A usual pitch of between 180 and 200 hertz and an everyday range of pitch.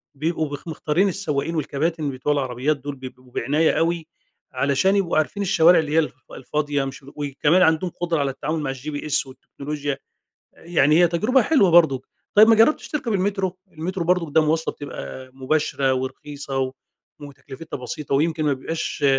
No: medium, 150 Hz; average, 3.5 semitones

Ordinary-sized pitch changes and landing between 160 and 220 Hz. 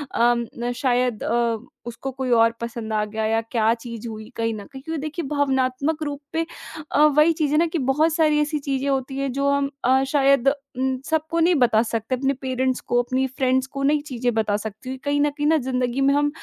No: average, 3.4 semitones; very high, 265 Hz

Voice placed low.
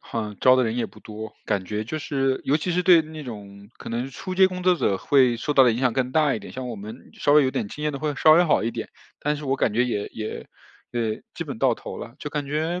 Yes: low, 130 Hz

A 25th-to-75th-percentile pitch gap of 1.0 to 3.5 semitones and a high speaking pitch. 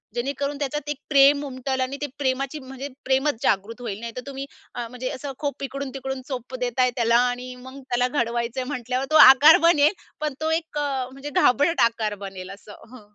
Yes: narrow, 2.4 semitones; very high, 260 Hz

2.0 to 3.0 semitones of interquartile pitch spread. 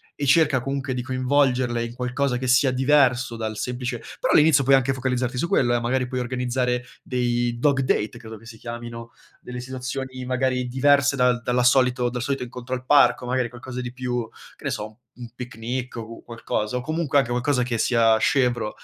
No: narrow, 1.4 semitones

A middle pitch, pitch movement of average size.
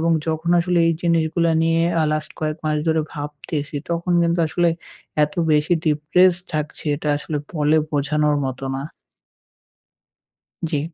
No: medium, 155 Hz; narrow, 2.0 semitones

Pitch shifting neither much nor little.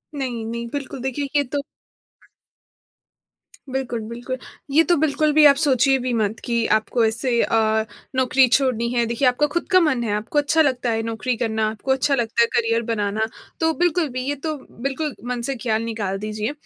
Yes: average, 3.6 semitones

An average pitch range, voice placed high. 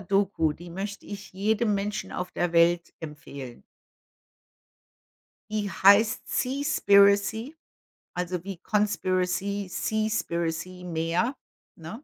Yes: average, 3.3 semitones; high, 195 Hz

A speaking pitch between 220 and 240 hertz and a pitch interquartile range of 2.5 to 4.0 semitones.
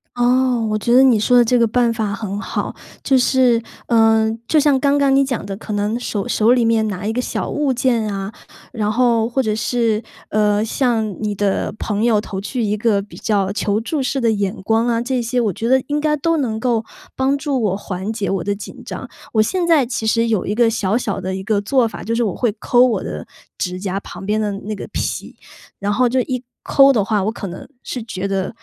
Yes: high, 225 Hz; average, 3.3 semitones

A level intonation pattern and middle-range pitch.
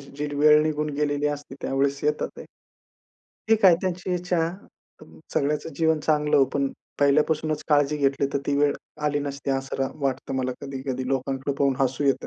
Yes: narrow, 1.7 semitones; medium, 145 Hz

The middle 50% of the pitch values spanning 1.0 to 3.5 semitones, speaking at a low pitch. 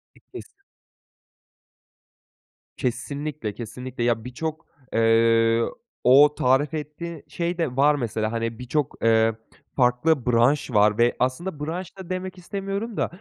No: wide, 5.6 semitones; low, 130 Hz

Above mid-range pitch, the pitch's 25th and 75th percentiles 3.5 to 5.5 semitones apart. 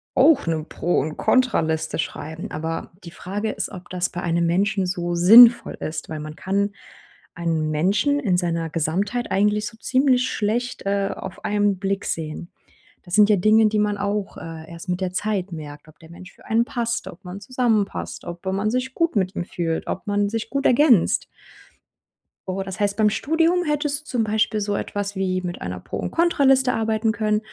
Yes: high, 200 Hz; average, 4.3 semitones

